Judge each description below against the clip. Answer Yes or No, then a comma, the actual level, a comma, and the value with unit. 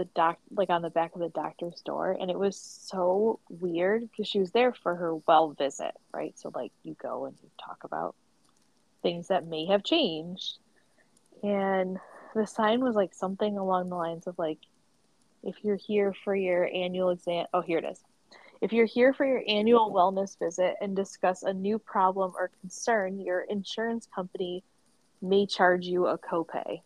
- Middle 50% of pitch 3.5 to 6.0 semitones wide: No, average, 2.7 semitones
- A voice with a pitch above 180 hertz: Yes, high, 190 Hz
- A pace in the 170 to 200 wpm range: Yes, average, 185 wpm